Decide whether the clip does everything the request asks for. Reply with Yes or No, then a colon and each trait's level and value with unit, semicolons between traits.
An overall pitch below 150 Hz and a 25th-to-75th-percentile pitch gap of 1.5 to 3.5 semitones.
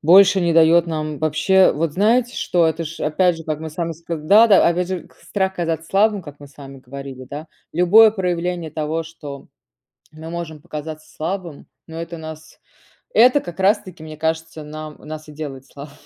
No: medium, 160 Hz; average, 2.7 semitones